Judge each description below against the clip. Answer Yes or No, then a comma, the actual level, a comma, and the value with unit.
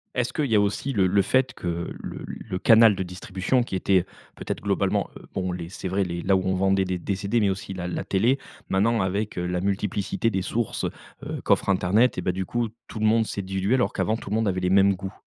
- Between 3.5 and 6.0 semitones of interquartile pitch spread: No, average, 2.8 semitones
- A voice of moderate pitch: No, very low, 95 Hz